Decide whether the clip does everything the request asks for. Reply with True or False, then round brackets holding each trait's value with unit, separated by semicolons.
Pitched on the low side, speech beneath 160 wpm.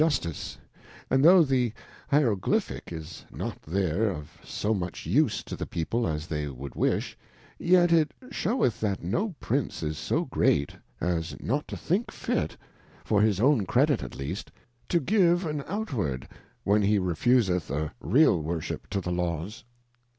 True (105 Hz; 150 wpm)